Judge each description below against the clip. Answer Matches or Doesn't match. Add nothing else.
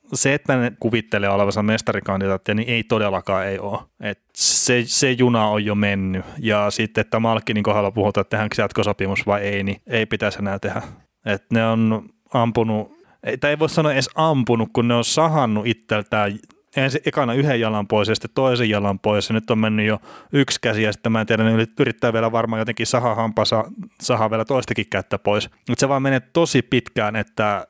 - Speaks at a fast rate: Matches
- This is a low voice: Matches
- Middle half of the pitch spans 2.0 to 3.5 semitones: Matches